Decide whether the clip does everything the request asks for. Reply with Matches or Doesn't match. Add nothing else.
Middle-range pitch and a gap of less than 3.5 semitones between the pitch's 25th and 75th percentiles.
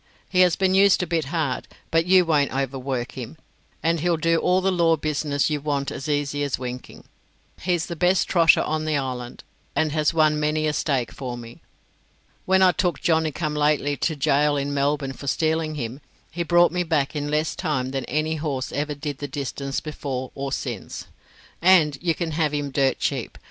Matches